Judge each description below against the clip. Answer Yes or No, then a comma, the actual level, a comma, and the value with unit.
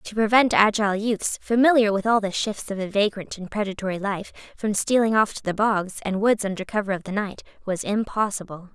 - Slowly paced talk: No, fast, 205 wpm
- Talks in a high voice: Yes, high, 205 Hz